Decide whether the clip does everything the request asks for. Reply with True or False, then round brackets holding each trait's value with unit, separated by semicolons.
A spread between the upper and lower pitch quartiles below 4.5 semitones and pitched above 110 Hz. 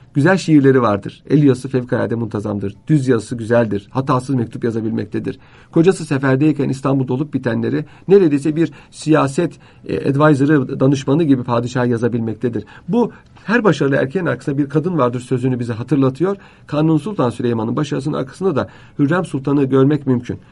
True (3.8 semitones; 135 Hz)